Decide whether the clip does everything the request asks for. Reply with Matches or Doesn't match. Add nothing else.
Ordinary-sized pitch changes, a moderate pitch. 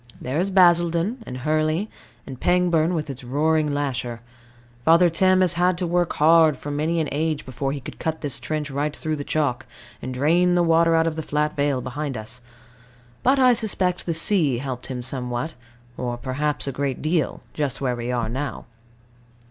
Matches